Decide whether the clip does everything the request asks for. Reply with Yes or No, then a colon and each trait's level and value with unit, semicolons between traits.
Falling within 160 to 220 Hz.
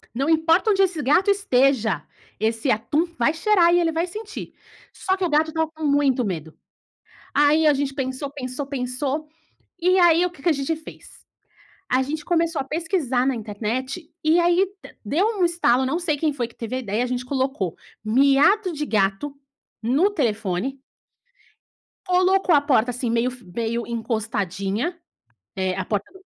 No: very high, 275 Hz